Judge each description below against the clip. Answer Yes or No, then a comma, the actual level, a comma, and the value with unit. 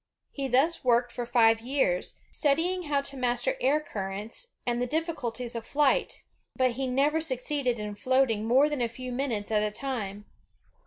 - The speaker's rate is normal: Yes, average, 175 wpm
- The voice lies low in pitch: No, very high, 250 Hz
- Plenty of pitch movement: No, average, 3.4 semitones